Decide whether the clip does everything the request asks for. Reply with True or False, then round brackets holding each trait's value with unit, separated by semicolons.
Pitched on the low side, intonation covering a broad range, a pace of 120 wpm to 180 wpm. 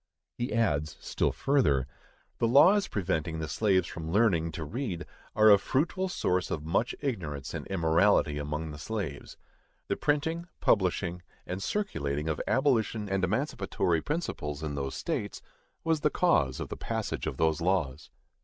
True (90 Hz; 7.5 semitones; 155 wpm)